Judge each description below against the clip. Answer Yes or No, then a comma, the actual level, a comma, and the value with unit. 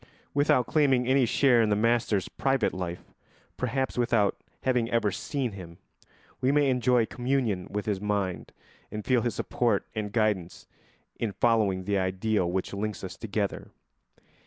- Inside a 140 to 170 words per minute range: Yes, average, 150 wpm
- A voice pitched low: Yes, low, 110 Hz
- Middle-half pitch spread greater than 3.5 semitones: Yes, average, 3.9 semitones